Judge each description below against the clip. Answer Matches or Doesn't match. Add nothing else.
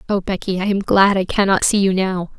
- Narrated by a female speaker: Matches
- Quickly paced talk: Matches